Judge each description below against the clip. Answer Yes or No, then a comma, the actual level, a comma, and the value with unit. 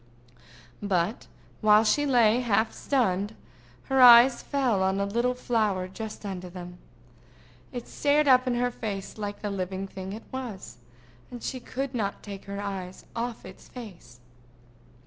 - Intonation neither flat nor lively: Yes, average, 4.1 semitones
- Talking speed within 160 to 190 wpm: No, average, 150 wpm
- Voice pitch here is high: Yes, high, 215 Hz